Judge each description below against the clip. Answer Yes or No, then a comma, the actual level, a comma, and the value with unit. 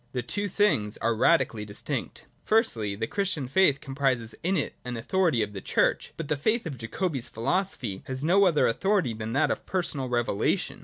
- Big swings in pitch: Yes, wide, 8.4 semitones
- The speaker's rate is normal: Yes, average, 190 wpm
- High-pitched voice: No, low, 135 Hz